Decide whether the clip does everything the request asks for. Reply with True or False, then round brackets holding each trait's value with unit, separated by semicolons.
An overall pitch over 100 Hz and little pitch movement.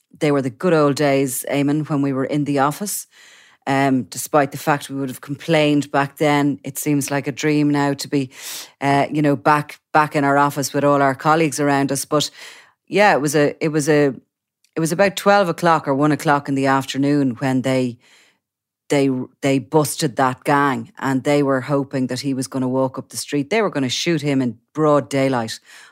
True (140 Hz; 1.7 semitones)